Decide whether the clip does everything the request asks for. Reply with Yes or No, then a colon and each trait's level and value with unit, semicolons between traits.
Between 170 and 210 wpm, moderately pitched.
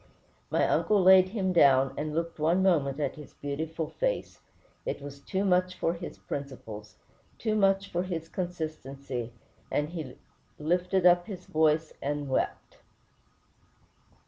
No: average, 140 wpm; medium, 165 Hz